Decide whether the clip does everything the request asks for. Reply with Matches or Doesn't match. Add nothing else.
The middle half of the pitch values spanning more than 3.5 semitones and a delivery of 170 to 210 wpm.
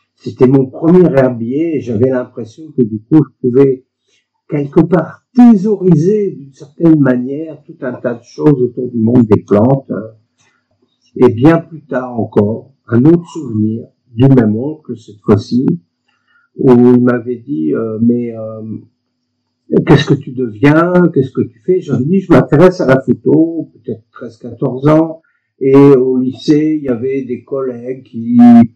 Doesn't match